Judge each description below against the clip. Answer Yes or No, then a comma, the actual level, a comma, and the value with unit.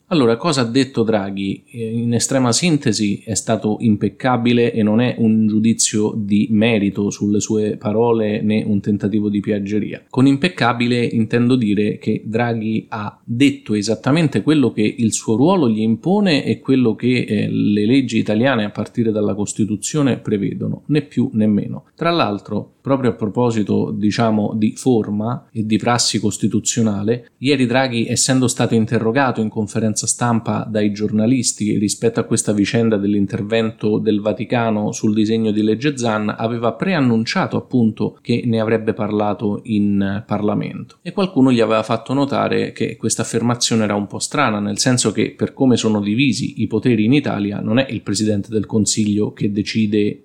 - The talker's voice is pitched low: Yes, low, 110 Hz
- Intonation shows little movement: Yes, narrow, 2.1 semitones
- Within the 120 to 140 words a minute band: No, average, 160 wpm